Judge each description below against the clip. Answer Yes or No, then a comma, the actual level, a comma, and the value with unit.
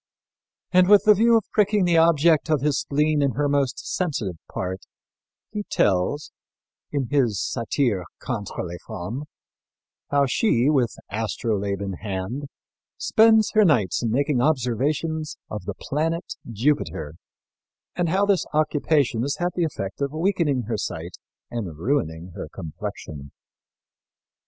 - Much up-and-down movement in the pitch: Yes, wide, 7.5 semitones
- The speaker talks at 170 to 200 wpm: No, slow, 135 wpm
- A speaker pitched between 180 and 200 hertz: No, medium, 140 Hz